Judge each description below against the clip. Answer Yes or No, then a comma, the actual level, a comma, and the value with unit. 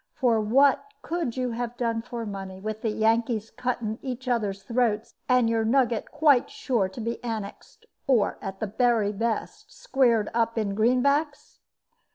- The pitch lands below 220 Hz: No, high, 230 Hz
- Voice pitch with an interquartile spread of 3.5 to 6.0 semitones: No, narrow, 2.6 semitones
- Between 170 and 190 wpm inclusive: No, average, 160 wpm